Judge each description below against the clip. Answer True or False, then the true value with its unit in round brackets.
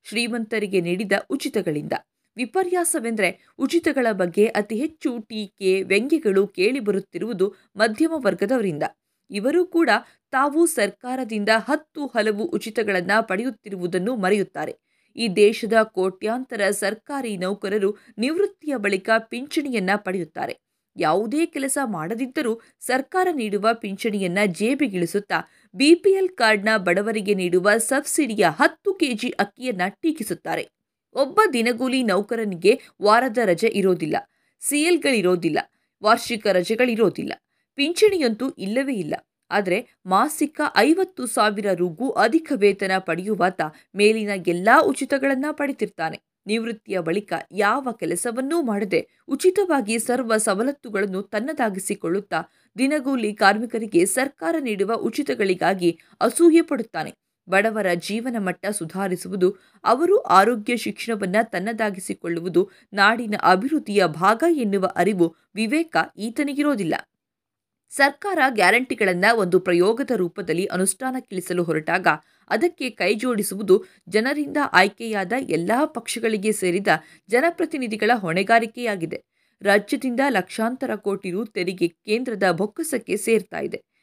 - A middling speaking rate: True (90 wpm)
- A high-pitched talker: True (220 Hz)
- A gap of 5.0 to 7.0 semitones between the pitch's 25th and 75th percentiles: True (5.5 semitones)